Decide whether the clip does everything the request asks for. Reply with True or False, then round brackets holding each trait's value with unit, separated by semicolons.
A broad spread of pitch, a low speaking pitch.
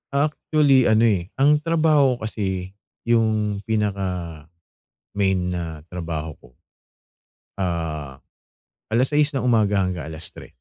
True (6.9 semitones; 105 Hz)